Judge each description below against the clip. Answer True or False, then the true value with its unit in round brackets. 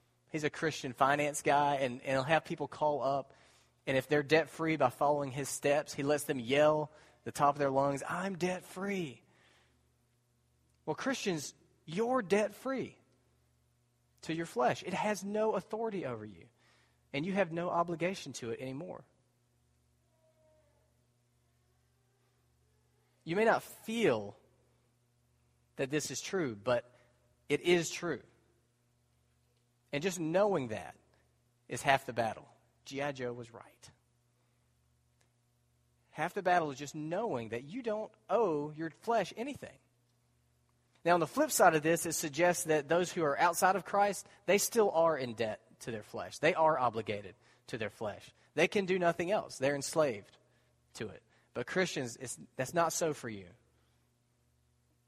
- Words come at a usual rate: True (150 wpm)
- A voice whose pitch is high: False (135 Hz)